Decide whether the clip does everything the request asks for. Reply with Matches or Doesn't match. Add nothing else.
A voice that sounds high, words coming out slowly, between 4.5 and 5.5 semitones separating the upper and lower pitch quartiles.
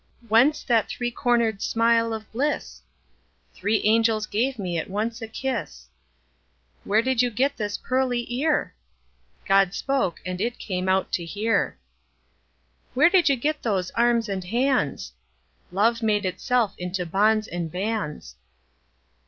Matches